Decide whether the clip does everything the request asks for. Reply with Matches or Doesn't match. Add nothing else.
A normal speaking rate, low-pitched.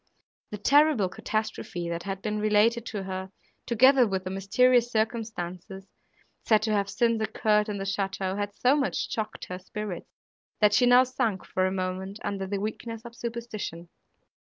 Doesn't match